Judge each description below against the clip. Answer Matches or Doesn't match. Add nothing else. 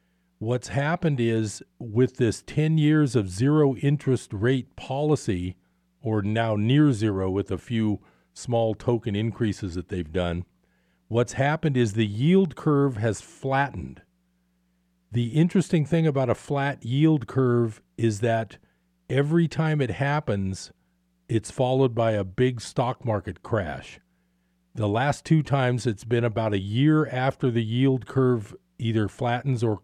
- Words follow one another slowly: Doesn't match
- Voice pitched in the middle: Doesn't match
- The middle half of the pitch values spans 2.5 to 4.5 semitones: Doesn't match